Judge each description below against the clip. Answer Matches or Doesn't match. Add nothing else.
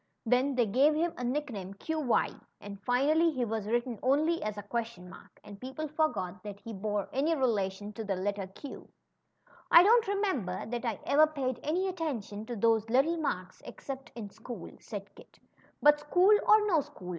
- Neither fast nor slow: Matches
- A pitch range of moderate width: Doesn't match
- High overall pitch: Matches